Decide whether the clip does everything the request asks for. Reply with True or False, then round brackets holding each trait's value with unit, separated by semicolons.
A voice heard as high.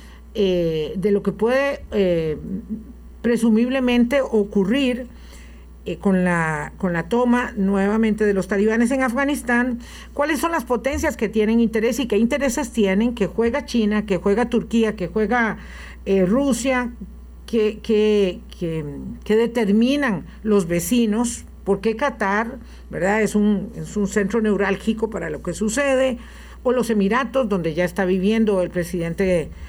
True (215 Hz)